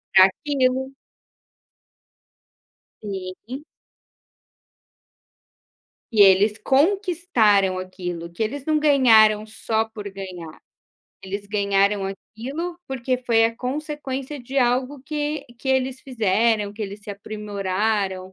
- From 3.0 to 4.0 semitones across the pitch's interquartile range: No, average, 4.9 semitones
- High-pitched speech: Yes, high, 220 Hz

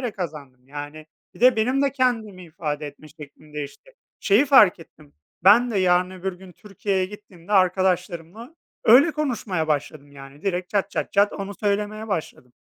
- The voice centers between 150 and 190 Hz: Yes, medium, 185 Hz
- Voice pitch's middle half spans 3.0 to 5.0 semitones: No, wide, 5.5 semitones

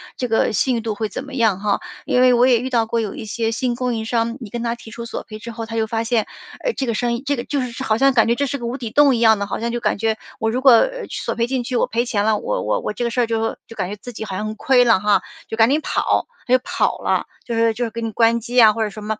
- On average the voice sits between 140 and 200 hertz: No, high, 230 Hz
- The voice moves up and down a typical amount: No, narrow, 2.0 semitones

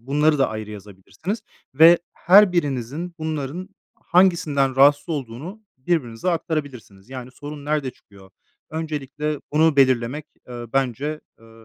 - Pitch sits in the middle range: Yes, medium, 145 Hz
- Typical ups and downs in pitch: Yes, average, 4.3 semitones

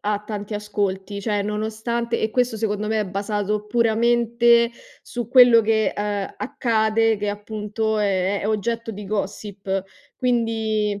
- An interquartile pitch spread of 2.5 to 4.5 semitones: No, narrow, 1.9 semitones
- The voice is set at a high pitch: Yes, high, 215 Hz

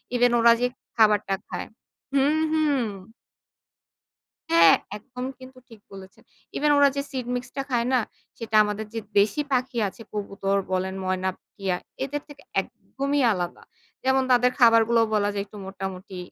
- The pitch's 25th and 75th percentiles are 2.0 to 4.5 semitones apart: No, average, 4.9 semitones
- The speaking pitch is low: No, high, 230 Hz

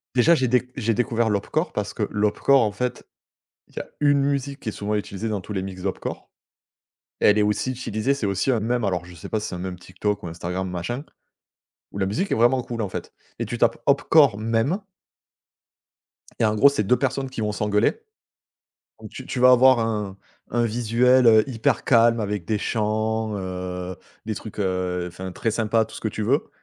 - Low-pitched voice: Yes, low, 110 Hz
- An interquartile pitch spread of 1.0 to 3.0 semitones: No, average, 3.8 semitones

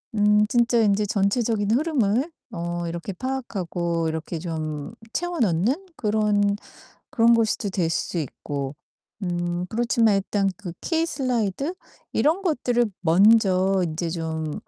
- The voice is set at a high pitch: Yes, high, 205 Hz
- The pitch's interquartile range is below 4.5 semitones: No, wide, 5.5 semitones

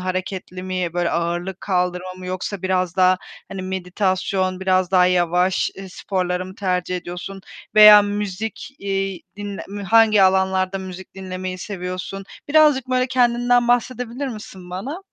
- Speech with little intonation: Yes, narrow, 2.0 semitones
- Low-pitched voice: No, high, 190 Hz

